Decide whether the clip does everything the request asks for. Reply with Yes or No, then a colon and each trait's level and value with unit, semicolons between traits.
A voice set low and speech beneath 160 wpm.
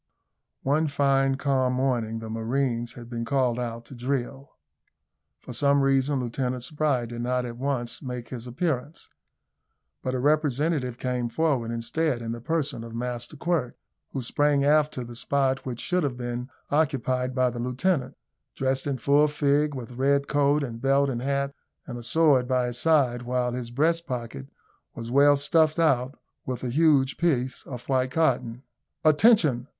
No: low, 130 Hz; average, 165 wpm